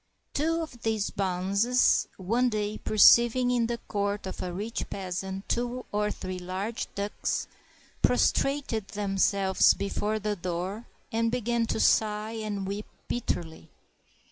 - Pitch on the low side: No, high, 210 Hz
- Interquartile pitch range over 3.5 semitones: No, average, 3.2 semitones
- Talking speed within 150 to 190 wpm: No, average, 140 wpm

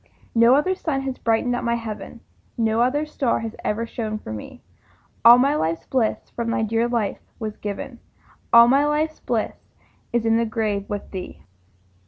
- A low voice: No, high, 230 Hz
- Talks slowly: No, average, 180 wpm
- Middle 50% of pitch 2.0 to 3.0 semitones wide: Yes, average, 2.7 semitones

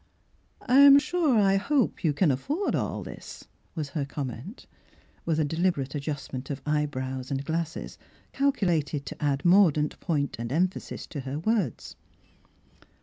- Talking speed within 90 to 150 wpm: Yes, average, 145 wpm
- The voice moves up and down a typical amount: No, wide, 5.7 semitones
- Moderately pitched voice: Yes, medium, 155 Hz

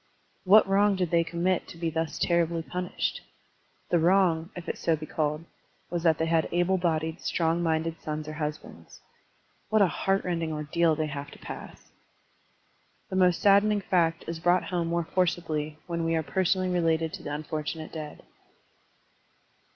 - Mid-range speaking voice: Yes, medium, 165 Hz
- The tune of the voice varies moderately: No, narrow, 2.1 semitones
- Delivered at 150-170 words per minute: Yes, average, 165 wpm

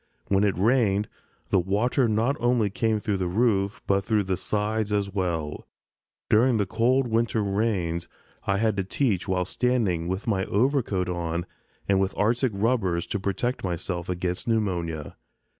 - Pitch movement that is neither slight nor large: Yes, average, 3.6 semitones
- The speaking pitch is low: Yes, low, 100 Hz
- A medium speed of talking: Yes, average, 155 wpm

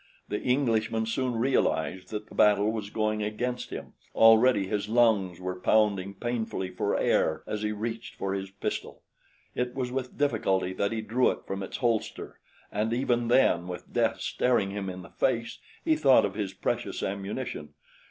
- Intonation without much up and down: No, average, 3.6 semitones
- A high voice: No, low, 110 Hz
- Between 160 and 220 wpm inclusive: Yes, average, 170 wpm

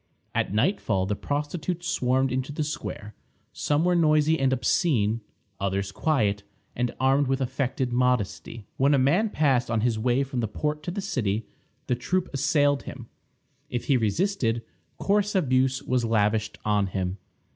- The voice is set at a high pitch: No, low, 130 Hz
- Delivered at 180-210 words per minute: No, average, 155 wpm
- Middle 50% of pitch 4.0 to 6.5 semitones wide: Yes, average, 4.7 semitones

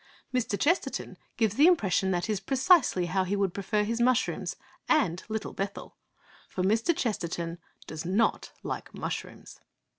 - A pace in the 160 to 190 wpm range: No, average, 150 wpm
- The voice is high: Yes, high, 205 Hz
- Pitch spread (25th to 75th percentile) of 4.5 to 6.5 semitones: Yes, average, 4.9 semitones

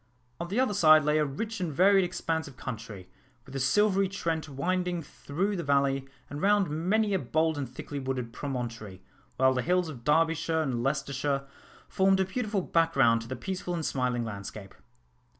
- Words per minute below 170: No, average, 180 wpm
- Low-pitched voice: No, medium, 150 Hz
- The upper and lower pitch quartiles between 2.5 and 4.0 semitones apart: No, wide, 5.6 semitones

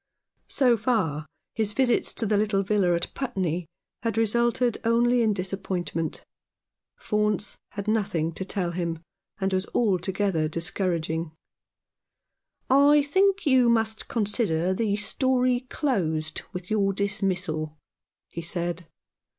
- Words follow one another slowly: Yes, slow, 120 wpm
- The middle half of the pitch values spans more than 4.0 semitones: Yes, average, 5.0 semitones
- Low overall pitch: No, high, 200 Hz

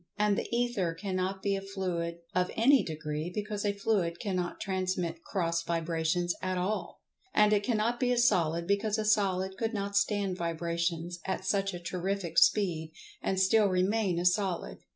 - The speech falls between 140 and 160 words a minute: No, average, 170 wpm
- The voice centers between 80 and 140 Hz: No, high, 190 Hz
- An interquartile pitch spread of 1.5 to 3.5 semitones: Yes, average, 3.2 semitones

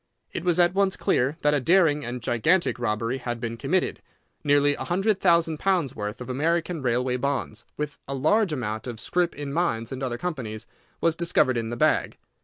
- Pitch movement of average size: No, wide, 6.0 semitones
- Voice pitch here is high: No, medium, 140 Hz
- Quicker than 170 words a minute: Yes, average, 195 wpm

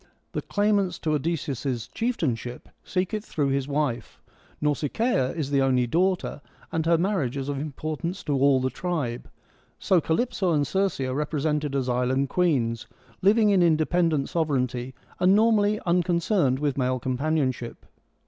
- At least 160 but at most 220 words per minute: No, average, 150 wpm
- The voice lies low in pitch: No, medium, 150 Hz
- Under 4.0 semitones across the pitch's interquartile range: No, average, 5.3 semitones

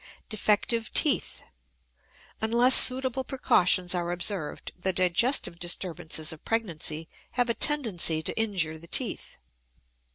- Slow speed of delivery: Yes, slow, 110 wpm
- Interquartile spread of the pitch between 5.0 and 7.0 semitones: Yes, wide, 5.5 semitones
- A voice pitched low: No, high, 190 Hz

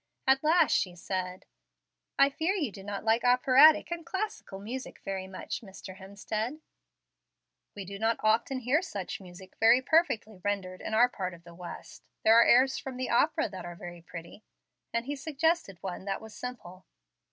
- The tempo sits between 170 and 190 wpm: Yes, average, 175 wpm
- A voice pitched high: Yes, high, 220 Hz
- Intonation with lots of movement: Yes, wide, 6.0 semitones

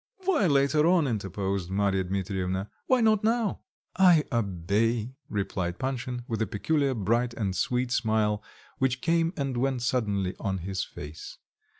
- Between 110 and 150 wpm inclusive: Yes, average, 140 wpm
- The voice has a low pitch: Yes, low, 115 Hz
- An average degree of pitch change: No, wide, 5.8 semitones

